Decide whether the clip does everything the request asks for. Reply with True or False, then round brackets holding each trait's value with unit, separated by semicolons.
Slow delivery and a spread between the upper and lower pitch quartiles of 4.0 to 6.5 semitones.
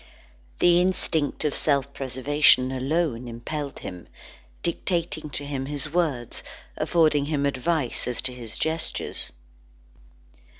False (115 wpm; 3.5 semitones)